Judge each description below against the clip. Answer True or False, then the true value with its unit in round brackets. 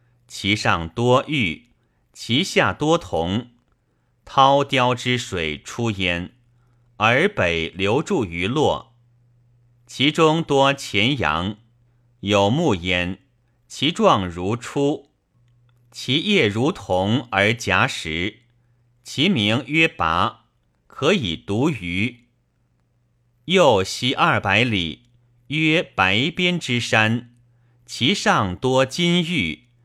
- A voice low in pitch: True (120 Hz)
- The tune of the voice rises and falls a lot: False (3.8 semitones)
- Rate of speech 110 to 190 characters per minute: True (125 characters per minute)